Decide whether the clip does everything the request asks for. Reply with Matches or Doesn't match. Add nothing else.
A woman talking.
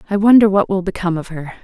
Matches